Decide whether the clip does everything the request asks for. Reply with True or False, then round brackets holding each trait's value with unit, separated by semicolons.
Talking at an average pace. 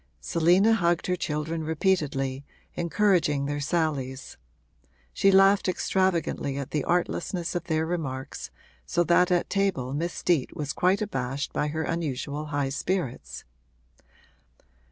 False (125 wpm)